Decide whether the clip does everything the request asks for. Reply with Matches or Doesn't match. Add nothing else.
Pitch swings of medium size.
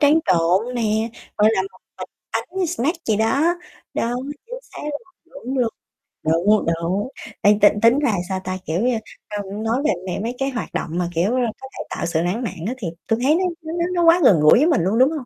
Doesn't match